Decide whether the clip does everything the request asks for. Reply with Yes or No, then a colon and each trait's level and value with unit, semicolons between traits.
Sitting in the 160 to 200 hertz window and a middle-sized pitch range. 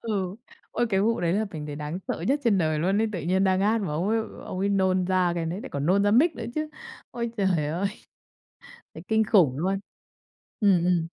Yes: high, 190 Hz; average, 3.7 semitones